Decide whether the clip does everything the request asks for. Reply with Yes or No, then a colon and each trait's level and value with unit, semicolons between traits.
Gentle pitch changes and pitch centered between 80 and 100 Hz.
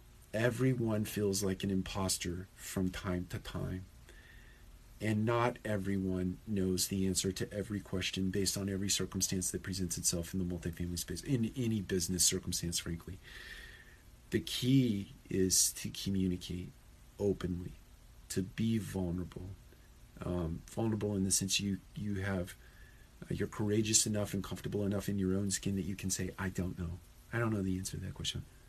Yes: narrow, 2.0 semitones; very low, 95 Hz